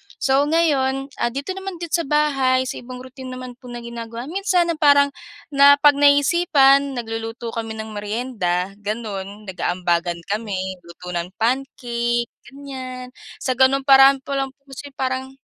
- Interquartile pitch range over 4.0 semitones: No, average, 3.7 semitones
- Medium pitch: No, very high, 255 Hz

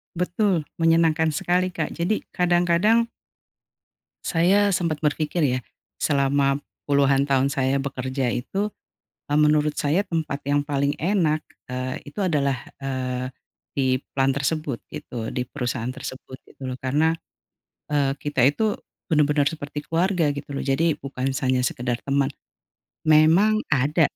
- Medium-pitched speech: Yes, medium, 145 Hz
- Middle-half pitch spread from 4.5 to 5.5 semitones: No, average, 3.6 semitones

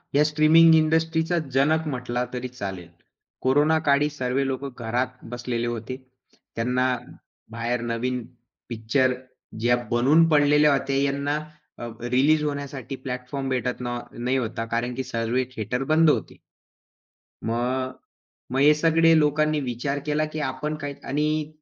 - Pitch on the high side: No, low, 135 Hz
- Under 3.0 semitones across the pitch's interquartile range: No, average, 3.5 semitones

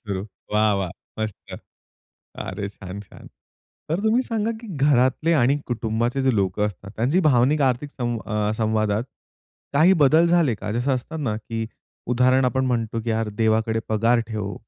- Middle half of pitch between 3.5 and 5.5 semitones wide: Yes, average, 4.2 semitones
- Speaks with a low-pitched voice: Yes, low, 120 Hz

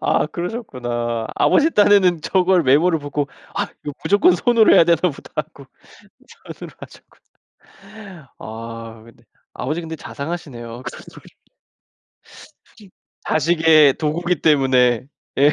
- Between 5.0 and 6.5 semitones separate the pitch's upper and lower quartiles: Yes, wide, 5.6 semitones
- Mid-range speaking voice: Yes, medium, 155 Hz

